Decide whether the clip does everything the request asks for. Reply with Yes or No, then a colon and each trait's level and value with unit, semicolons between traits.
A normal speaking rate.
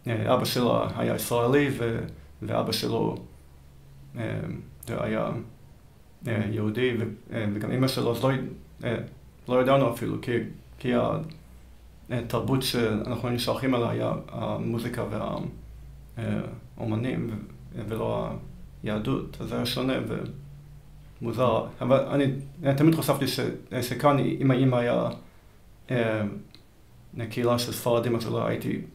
No: slow, 95 wpm